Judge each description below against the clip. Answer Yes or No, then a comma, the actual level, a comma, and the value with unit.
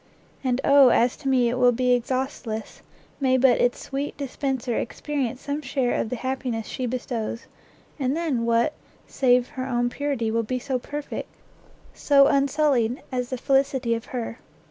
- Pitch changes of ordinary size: No, narrow, 2.2 semitones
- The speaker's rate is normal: Yes, average, 165 wpm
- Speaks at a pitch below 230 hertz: No, very high, 255 Hz